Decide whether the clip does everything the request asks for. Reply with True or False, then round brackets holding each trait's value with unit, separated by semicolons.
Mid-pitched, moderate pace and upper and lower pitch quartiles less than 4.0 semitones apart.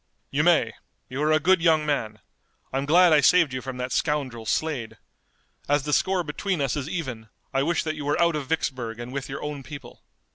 False (145 Hz; 215 wpm; 3.5 semitones)